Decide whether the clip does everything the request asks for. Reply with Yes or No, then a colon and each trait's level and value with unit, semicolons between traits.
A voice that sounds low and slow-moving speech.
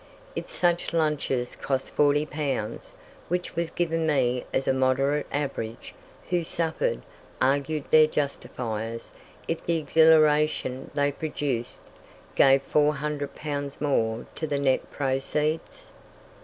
No: medium, 145 Hz; slow, 115 wpm